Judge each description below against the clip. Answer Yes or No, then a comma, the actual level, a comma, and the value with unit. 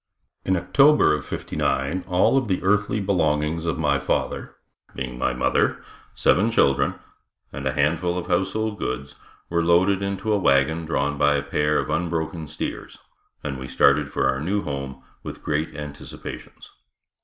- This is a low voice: Yes, very low, 80 Hz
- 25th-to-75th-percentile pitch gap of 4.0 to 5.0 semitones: Yes, average, 4.7 semitones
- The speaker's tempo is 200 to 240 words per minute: No, average, 155 wpm